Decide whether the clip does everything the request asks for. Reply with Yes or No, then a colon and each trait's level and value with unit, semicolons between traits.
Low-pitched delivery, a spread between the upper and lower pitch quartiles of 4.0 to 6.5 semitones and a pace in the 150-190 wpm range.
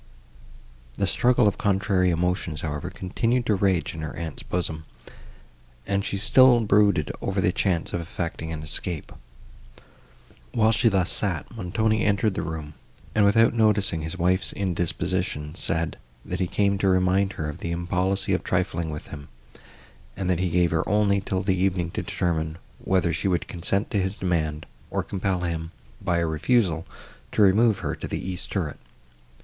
No: very low, 90 Hz; average, 3.1 semitones; average, 170 wpm